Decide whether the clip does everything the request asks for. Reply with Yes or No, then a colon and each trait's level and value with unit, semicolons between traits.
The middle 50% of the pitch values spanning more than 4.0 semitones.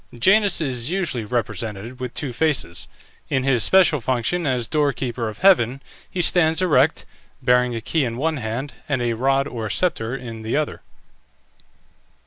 Yes: average, 4.8 semitones